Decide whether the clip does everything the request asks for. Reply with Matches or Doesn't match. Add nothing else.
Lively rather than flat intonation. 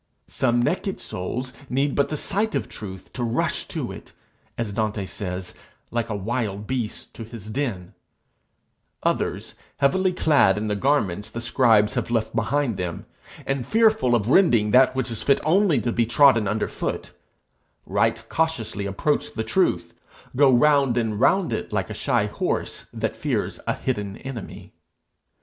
Doesn't match